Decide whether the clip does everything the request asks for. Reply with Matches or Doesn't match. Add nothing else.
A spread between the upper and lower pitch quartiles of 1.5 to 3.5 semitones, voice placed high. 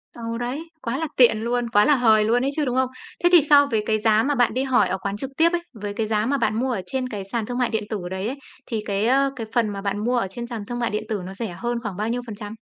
Matches